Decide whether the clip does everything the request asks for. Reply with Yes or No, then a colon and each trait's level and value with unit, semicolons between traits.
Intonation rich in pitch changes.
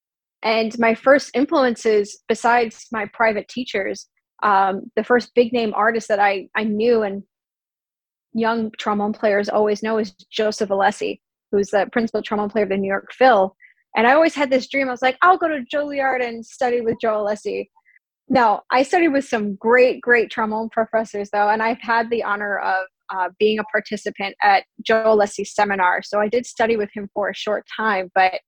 No: average, 2.8 semitones